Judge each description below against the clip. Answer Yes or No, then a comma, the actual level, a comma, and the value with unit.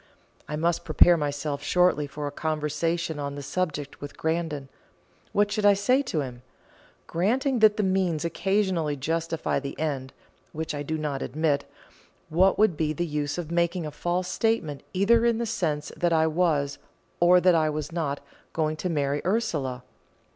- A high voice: No, medium, 160 Hz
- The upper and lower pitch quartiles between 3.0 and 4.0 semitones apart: Yes, average, 3.6 semitones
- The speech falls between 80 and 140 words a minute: No, average, 170 wpm